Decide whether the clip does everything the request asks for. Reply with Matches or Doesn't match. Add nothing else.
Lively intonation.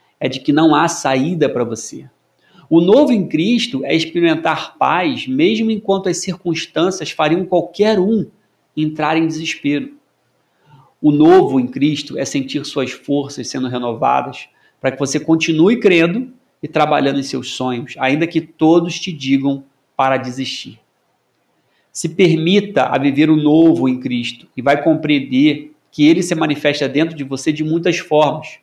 Doesn't match